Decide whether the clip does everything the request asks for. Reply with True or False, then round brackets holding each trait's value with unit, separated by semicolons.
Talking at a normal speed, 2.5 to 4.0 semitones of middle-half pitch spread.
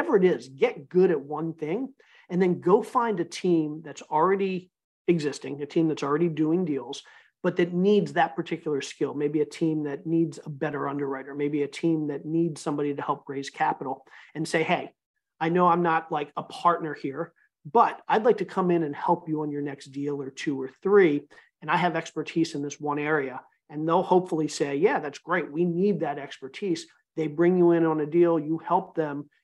False (210 wpm; 3.1 semitones)